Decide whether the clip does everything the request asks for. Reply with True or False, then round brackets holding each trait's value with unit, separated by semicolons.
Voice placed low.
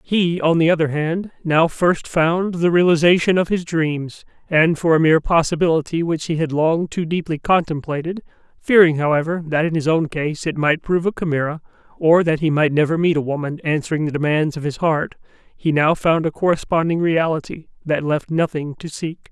False (160 Hz)